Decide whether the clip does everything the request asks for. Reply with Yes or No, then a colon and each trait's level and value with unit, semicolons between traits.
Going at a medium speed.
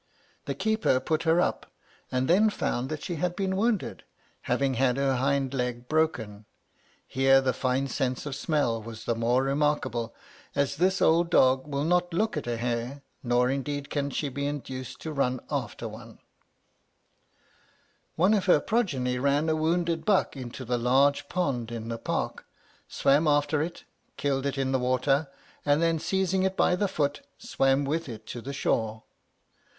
Yes: average, 170 wpm